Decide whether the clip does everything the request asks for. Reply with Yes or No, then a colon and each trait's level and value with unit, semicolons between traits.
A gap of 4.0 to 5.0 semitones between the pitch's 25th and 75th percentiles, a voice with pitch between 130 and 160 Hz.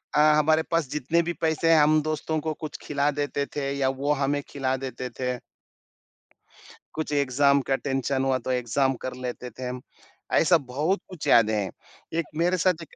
No: average, 3.3 semitones; medium, 140 Hz